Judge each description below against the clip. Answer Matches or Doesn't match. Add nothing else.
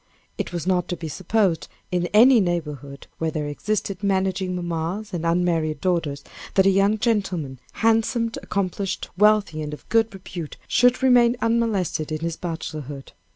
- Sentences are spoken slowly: Doesn't match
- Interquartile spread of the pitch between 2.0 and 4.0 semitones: Doesn't match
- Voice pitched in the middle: Matches